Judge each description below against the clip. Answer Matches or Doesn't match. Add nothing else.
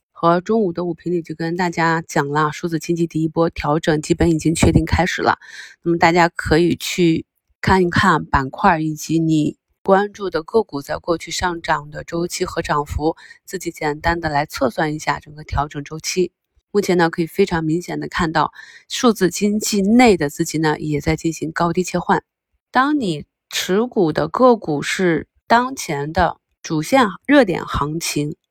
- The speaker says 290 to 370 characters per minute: Doesn't match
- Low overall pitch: Doesn't match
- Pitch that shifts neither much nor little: Matches